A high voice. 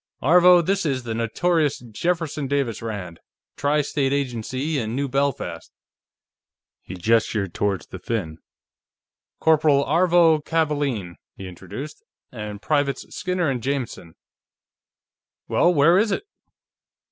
No: medium, 140 Hz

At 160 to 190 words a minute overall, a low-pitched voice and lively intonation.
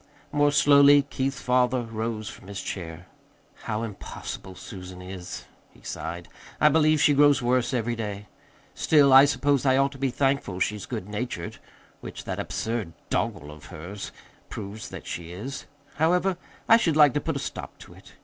Yes: average, 170 wpm; low, 120 Hz; wide, 6.2 semitones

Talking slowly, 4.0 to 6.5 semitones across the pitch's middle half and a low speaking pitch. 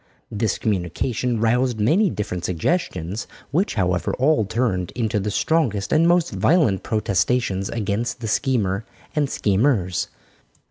Yes: slow, 125 wpm; average, 5.2 semitones; low, 110 Hz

